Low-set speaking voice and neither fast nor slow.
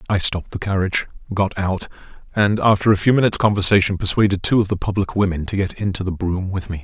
No: very low, 95 Hz; fast, 220 wpm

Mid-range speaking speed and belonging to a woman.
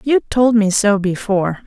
Yes: average, 180 wpm; female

